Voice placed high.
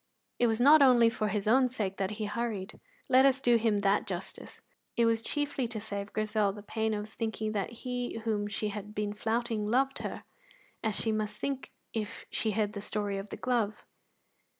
Yes: high, 220 Hz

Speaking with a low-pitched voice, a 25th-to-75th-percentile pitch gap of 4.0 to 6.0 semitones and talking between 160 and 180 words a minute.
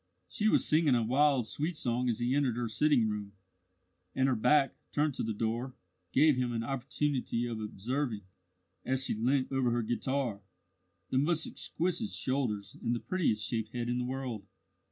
No: low, 125 Hz; average, 3.5 semitones; average, 175 wpm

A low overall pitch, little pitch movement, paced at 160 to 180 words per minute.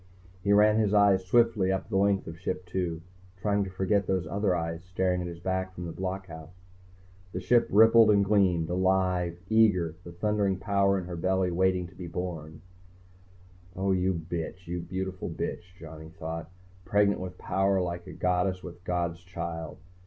Yes: very low, 95 Hz; narrow, 2.1 semitones; average, 175 wpm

